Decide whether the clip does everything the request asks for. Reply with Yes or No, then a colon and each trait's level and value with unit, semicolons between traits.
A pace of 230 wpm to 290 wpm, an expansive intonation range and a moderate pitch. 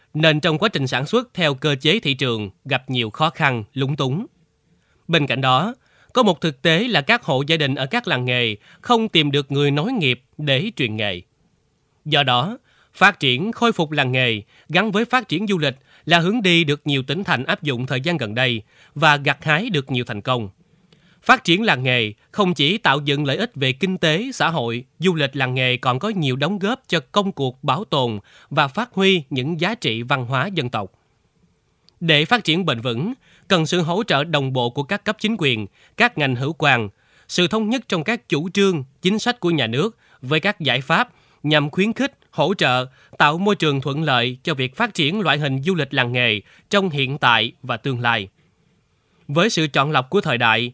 No: average, 220 wpm; wide, 6.0 semitones; medium, 150 Hz